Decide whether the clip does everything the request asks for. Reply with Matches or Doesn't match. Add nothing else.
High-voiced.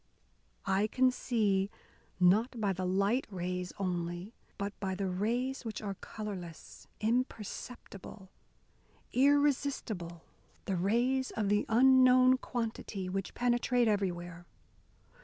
Matches